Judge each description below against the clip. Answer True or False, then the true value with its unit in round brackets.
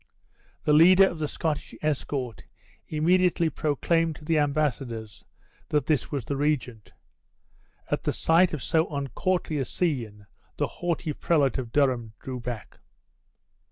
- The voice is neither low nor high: True (150 Hz)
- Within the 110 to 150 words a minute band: True (135 wpm)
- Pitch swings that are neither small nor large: True (4.1 semitones)